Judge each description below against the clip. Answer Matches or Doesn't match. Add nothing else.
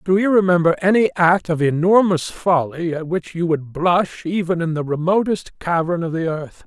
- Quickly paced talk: Doesn't match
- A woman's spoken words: Doesn't match